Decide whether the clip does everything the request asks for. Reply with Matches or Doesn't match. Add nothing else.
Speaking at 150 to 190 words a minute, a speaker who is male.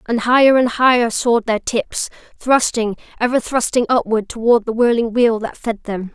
Doesn't match